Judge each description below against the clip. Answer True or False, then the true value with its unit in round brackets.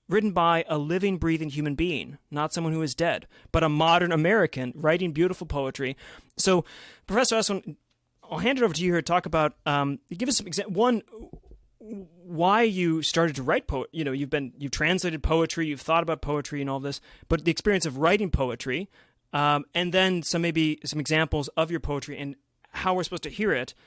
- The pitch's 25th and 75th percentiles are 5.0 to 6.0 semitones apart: False (3.5 semitones)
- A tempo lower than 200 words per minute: False (205 wpm)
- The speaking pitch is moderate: True (165 Hz)